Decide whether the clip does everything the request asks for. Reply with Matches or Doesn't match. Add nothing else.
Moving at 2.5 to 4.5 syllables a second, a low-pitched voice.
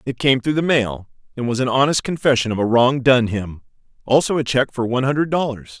Doesn't match